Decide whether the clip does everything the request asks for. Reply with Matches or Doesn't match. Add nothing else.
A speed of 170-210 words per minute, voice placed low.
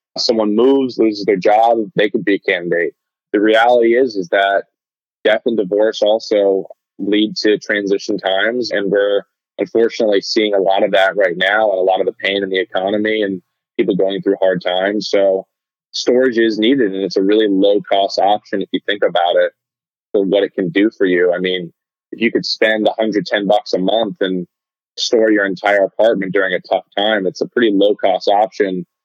Matches